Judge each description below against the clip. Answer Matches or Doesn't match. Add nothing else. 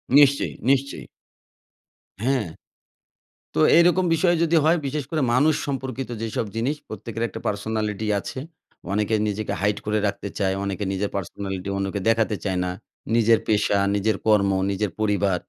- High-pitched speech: Doesn't match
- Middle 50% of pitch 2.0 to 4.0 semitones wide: Doesn't match